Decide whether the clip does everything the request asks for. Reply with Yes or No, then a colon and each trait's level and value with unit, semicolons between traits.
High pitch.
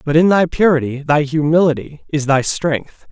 No: medium, 150 Hz